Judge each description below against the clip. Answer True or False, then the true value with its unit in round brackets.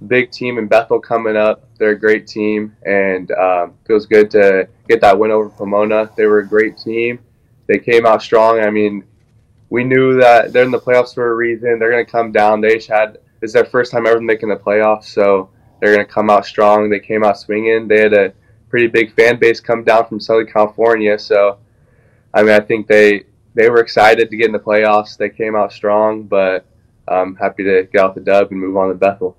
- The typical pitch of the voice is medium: False (110 Hz)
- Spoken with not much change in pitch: True (2.0 semitones)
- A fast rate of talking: True (225 wpm)